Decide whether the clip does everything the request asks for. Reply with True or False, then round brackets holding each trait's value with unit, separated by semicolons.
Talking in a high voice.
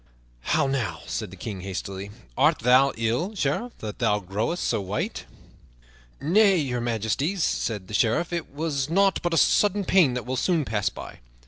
False (130 Hz)